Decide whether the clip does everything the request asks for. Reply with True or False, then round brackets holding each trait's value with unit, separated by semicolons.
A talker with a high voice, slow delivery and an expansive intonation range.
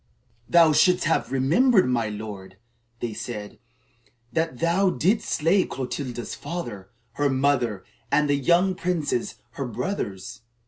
False (140 Hz; 125 wpm; 6.6 semitones)